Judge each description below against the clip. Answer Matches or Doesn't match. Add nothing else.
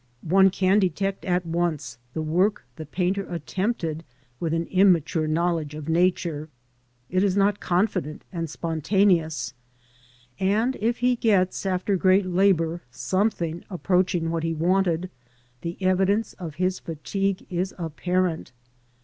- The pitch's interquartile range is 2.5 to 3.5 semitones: Matches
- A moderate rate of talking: Doesn't match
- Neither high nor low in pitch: Matches